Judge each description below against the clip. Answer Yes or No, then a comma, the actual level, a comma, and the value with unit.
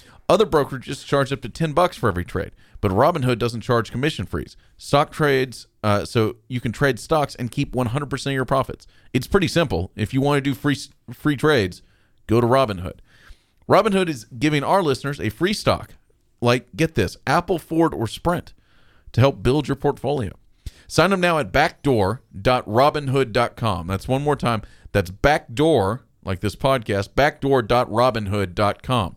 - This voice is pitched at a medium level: No, low, 130 Hz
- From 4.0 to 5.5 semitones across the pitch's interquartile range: Yes, average, 4.8 semitones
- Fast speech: No, average, 165 wpm